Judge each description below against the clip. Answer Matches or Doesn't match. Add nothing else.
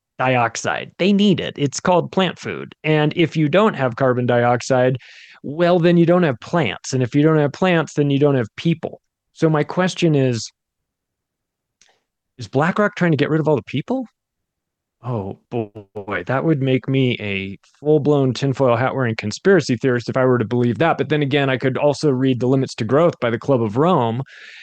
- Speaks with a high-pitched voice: Doesn't match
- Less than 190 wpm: Doesn't match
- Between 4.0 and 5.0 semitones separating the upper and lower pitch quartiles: Matches